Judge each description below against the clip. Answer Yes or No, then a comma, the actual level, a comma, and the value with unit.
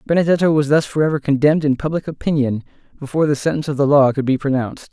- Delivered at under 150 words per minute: No, fast, 205 wpm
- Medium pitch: Yes, medium, 145 Hz